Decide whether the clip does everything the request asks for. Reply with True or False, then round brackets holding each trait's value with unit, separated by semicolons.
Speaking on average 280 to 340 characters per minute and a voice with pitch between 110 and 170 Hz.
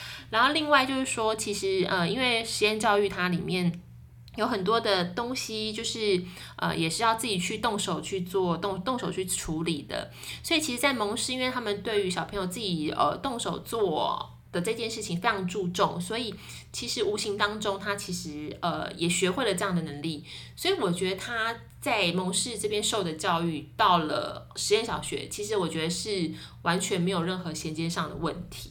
False (285 characters per minute; 195 Hz)